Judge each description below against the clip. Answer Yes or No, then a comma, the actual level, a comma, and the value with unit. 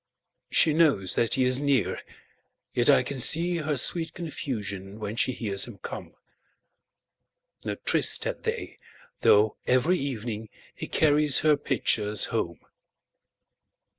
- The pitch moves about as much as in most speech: No, wide, 5.8 semitones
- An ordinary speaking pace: No, slow, 115 wpm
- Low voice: Yes, low, 125 Hz